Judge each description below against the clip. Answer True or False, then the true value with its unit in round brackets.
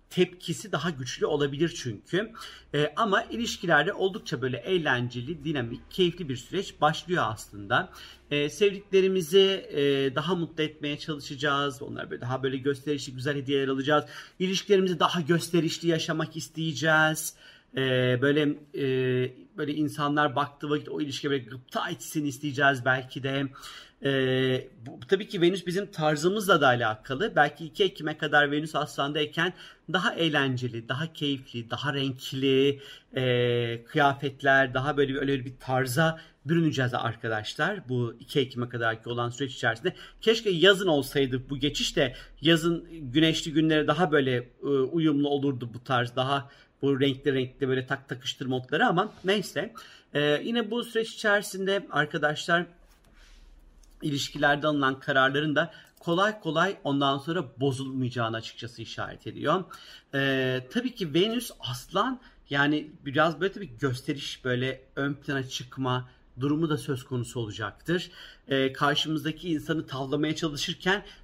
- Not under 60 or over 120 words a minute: False (135 wpm)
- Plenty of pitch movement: False (4.0 semitones)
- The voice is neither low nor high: True (145 Hz)